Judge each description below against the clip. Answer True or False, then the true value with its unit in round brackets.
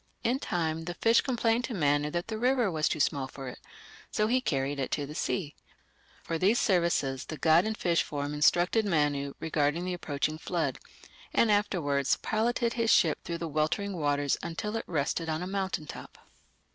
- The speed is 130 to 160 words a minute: False (185 wpm)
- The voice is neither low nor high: True (165 Hz)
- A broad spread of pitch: True (6.1 semitones)